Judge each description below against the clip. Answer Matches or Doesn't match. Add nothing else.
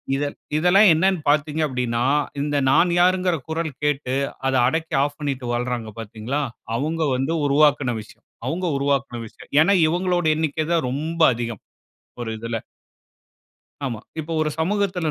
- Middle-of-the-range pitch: Matches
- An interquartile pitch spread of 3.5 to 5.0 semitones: Matches